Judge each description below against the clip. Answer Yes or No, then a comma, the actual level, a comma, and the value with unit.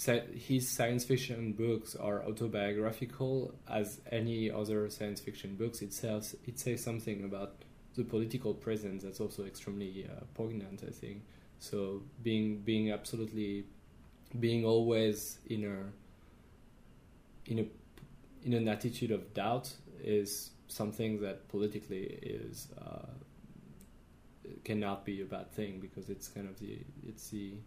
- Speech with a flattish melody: Yes, narrow, 2.3 semitones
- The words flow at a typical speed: No, slow, 130 wpm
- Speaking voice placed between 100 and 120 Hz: Yes, low, 105 Hz